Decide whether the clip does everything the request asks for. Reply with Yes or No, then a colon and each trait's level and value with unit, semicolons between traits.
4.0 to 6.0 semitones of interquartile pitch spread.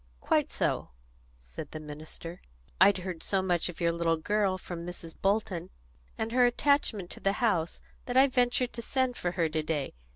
Yes: wide, 5.4 semitones